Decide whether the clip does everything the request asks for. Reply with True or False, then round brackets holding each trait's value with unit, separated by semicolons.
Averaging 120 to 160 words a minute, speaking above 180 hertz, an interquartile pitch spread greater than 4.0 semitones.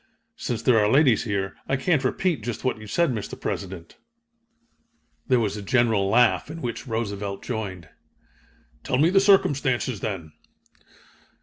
False (145 wpm; 115 Hz; 4.6 semitones)